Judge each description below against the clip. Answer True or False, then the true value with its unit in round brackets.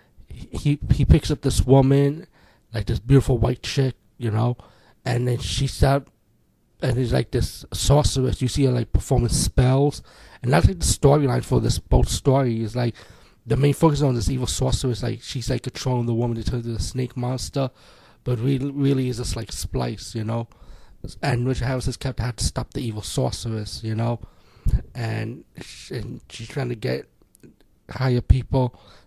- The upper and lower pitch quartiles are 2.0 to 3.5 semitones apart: True (2.9 semitones)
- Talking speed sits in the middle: True (180 wpm)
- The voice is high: False (125 Hz)